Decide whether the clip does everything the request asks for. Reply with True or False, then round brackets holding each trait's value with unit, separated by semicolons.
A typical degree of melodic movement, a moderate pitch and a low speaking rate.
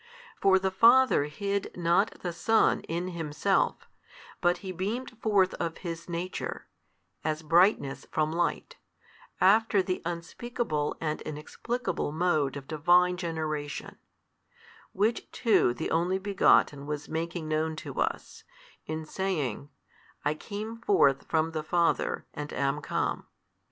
True (3.8 semitones; 170 Hz; 125 wpm)